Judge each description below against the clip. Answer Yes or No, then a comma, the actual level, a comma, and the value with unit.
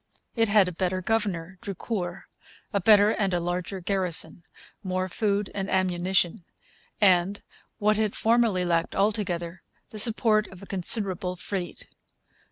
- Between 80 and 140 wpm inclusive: Yes, slow, 135 wpm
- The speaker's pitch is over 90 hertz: Yes, high, 190 Hz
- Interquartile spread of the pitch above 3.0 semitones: No, average, 2.7 semitones